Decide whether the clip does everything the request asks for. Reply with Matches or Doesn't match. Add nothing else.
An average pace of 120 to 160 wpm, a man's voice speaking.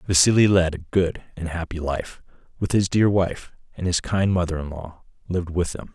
Doesn't match